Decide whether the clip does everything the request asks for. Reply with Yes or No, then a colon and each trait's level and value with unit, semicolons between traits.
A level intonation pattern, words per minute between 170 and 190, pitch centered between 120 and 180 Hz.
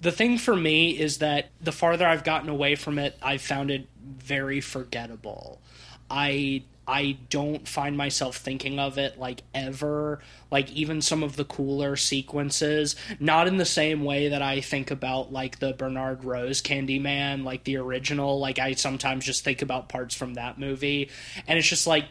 Yes: narrow, 2.0 semitones; average, 180 wpm; medium, 140 Hz